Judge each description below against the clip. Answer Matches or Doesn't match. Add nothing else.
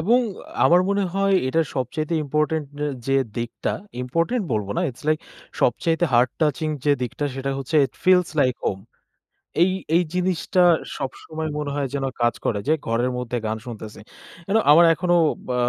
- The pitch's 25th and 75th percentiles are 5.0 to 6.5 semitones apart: Matches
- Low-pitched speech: Doesn't match